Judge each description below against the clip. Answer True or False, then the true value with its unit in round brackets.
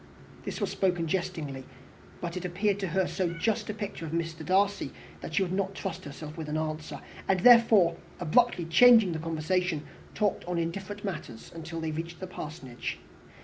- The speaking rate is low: False (180 wpm)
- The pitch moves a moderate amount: True (3.2 semitones)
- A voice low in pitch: False (175 Hz)